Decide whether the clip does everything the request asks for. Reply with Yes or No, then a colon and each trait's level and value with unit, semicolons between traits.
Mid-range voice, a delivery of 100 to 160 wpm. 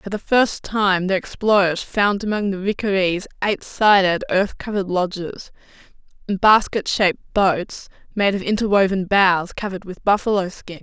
No: high, 195 Hz; average, 150 wpm